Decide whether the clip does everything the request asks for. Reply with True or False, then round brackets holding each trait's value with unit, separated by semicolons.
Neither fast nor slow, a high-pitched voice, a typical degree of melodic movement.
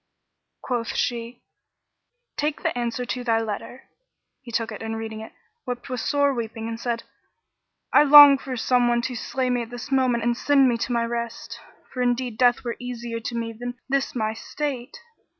False (185 wpm; 240 Hz; 1.7 semitones)